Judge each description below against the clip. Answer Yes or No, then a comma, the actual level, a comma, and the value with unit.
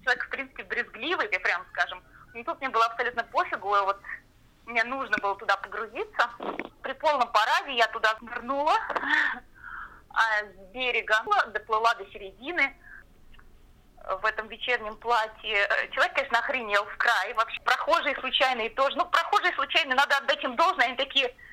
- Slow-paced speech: No, average, 150 wpm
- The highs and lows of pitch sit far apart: No, average, 4.3 semitones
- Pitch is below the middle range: No, high, 245 Hz